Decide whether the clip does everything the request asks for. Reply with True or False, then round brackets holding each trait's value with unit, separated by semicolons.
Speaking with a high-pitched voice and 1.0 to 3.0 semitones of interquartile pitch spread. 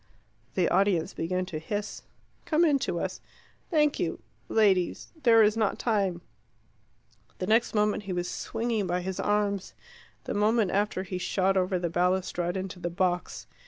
True (195 Hz; 2.7 semitones)